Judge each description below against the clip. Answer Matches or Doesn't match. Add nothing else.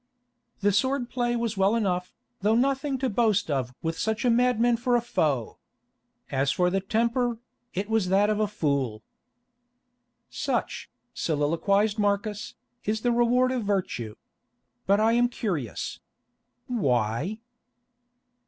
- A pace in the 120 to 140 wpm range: Matches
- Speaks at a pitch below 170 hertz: Doesn't match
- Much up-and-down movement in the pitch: Doesn't match